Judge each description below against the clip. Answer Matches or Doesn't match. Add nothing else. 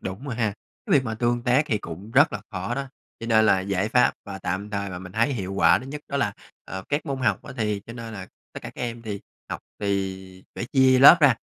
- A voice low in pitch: Matches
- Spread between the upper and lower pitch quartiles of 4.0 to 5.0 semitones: Matches